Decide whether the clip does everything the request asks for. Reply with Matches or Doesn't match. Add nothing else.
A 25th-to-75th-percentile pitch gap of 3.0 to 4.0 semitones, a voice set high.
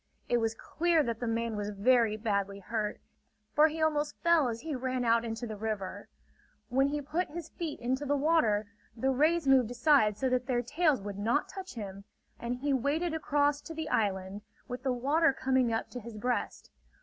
Doesn't match